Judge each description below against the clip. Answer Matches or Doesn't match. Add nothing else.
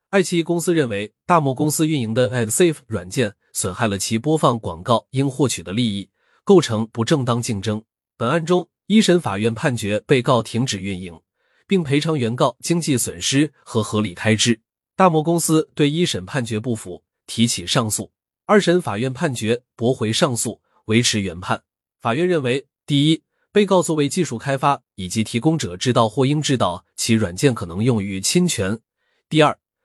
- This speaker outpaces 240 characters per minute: Matches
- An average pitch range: Doesn't match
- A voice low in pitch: Matches